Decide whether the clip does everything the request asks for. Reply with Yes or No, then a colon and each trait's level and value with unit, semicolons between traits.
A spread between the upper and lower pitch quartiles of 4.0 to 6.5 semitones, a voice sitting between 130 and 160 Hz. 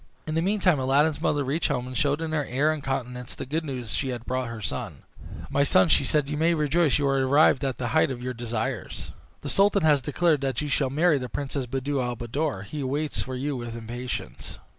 No: average, 3.3 semitones; low, 135 Hz